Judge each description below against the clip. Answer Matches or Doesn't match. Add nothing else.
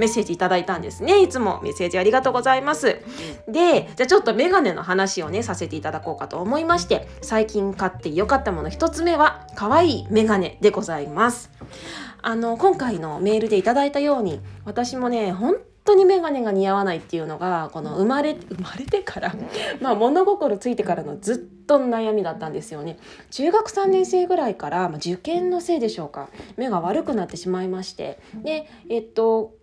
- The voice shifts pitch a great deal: Matches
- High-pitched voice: Matches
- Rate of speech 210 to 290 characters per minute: Doesn't match